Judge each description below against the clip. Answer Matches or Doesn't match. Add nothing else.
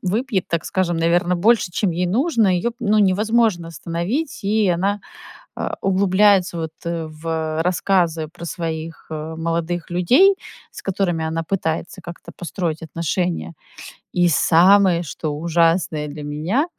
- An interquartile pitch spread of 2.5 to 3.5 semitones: Matches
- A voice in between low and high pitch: Matches